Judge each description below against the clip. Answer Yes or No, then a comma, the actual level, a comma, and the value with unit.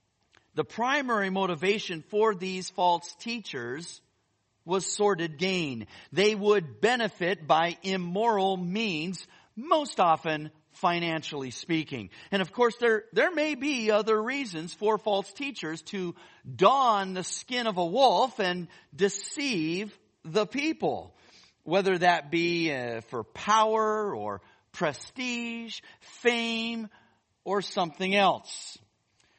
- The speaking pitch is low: No, high, 190 Hz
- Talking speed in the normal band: No, slow, 110 wpm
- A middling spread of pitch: Yes, average, 4.9 semitones